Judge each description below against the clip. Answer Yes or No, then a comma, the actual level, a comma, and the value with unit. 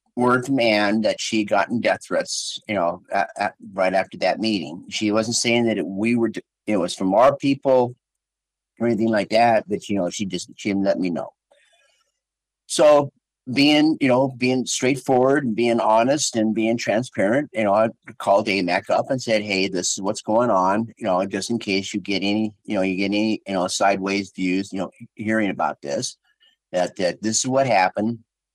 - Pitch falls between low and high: No, low, 110 Hz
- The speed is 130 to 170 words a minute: No, average, 200 wpm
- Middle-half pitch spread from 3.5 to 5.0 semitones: Yes, average, 3.8 semitones